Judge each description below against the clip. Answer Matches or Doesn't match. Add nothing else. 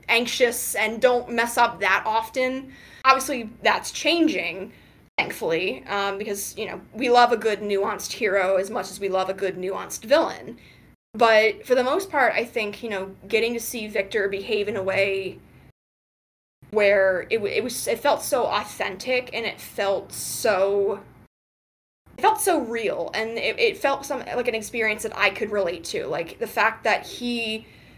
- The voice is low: Doesn't match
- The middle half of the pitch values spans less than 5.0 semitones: Matches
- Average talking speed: Matches